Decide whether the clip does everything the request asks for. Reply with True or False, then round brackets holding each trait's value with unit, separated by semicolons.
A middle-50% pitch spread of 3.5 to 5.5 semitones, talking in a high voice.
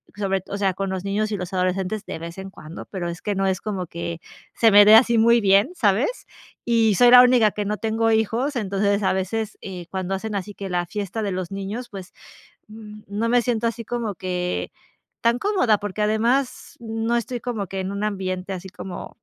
False (2.9 semitones; 205 Hz)